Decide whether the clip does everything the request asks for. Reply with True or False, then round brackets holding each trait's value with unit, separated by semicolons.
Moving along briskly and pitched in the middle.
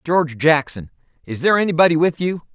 False (165 wpm; 160 Hz)